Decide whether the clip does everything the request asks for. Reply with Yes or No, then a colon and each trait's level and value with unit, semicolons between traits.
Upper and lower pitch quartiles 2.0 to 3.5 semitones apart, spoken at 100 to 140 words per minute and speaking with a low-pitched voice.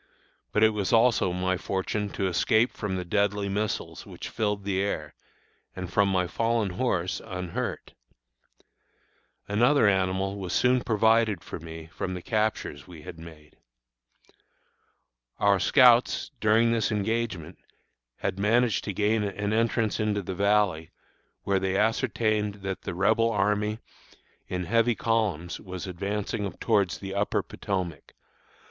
Yes: average, 2.9 semitones; slow, 135 wpm; low, 100 Hz